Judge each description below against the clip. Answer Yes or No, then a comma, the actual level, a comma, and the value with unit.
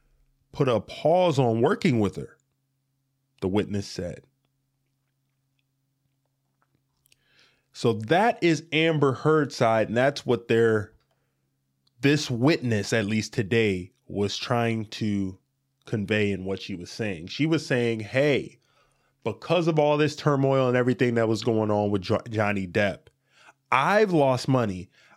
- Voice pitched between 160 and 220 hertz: No, low, 125 Hz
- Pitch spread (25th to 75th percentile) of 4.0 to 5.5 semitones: Yes, average, 4.4 semitones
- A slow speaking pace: Yes, slow, 130 wpm